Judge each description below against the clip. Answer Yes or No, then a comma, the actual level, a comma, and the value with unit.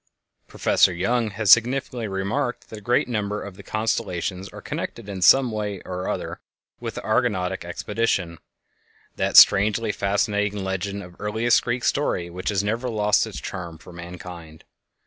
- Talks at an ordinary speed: Yes, average, 150 wpm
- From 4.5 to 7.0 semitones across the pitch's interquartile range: No, average, 3.4 semitones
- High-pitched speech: No, low, 100 Hz